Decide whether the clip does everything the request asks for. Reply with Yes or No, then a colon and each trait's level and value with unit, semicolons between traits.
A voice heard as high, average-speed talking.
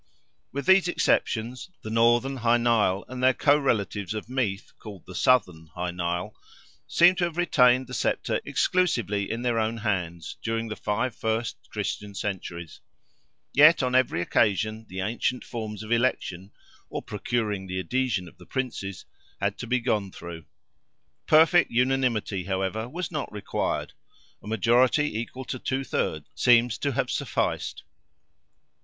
No: low, 115 Hz; average, 150 wpm